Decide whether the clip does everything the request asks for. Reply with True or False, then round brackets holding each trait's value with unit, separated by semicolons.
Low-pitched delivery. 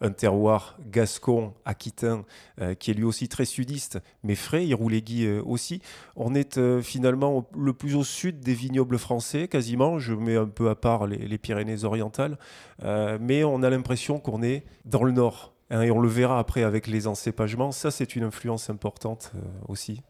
True (115 Hz)